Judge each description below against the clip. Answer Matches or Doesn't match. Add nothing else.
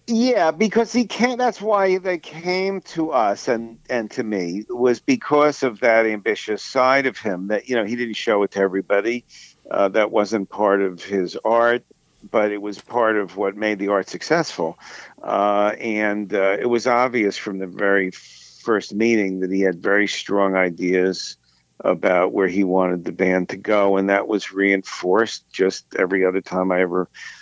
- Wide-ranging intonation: Doesn't match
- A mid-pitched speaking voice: Doesn't match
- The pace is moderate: Matches